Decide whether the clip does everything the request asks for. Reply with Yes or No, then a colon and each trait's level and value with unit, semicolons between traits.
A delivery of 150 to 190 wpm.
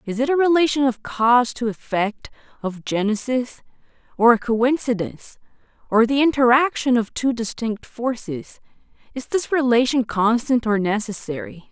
No: slow, 135 wpm